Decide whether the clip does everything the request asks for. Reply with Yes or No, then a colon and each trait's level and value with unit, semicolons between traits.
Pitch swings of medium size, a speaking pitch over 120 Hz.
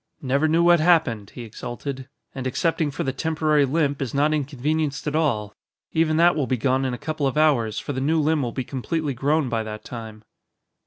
Yes: average, 3.6 semitones; medium, 140 Hz